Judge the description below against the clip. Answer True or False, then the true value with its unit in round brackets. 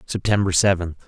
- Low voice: True (90 Hz)